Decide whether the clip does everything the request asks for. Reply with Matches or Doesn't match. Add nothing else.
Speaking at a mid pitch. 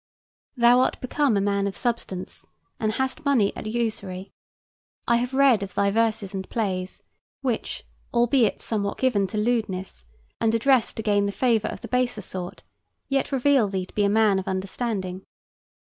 Doesn't match